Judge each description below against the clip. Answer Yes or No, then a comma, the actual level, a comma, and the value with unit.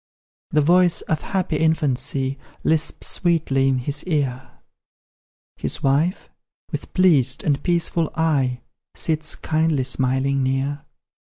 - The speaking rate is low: Yes, slow, 110 wpm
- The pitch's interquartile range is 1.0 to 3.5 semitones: Yes, average, 3.2 semitones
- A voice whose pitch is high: No, medium, 145 Hz